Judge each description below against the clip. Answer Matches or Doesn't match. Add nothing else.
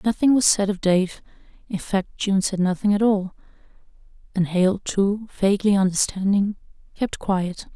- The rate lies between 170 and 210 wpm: Doesn't match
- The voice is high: Matches